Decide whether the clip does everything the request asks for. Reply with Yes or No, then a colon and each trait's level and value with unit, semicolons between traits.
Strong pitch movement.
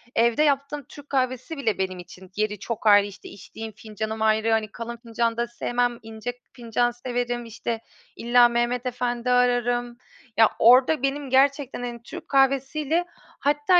No: average, 2.9 semitones